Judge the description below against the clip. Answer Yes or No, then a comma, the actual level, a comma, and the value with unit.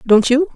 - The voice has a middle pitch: No, very high, 270 Hz